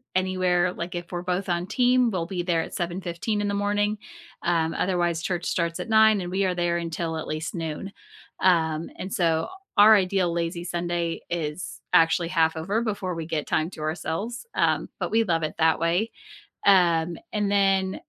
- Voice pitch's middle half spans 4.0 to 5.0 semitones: No, average, 2.8 semitones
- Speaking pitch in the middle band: Yes, medium, 175 Hz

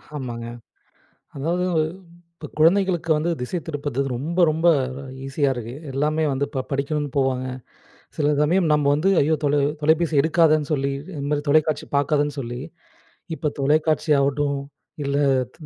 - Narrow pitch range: Yes, narrow, 2.3 semitones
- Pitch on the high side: No, medium, 150 Hz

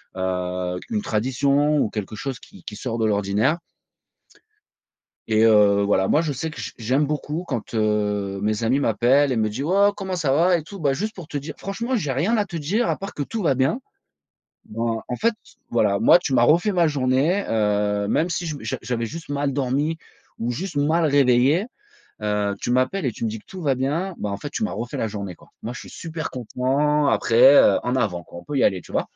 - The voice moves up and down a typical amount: No, wide, 6.7 semitones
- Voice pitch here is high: No, low, 135 Hz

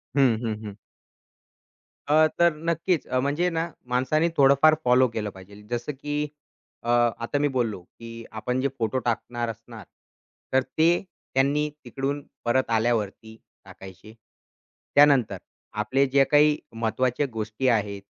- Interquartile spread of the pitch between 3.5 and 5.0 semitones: Yes, average, 4.5 semitones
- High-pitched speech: No, low, 125 Hz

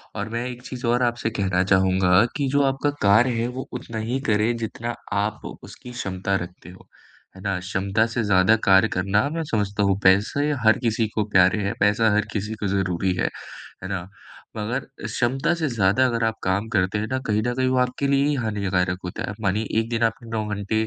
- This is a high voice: No, low, 110 Hz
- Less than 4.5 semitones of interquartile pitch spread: Yes, average, 3.6 semitones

